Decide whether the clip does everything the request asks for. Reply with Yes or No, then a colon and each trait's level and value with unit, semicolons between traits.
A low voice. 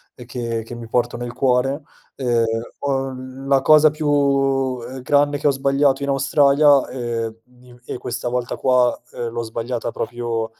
Yes: low, 130 Hz